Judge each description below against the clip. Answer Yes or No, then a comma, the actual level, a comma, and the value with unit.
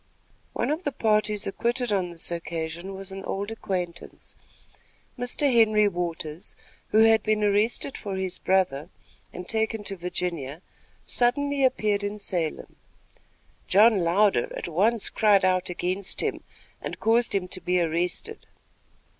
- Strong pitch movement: No, average, 3.7 semitones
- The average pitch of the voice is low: No, high, 195 Hz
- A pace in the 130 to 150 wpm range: Yes, average, 140 wpm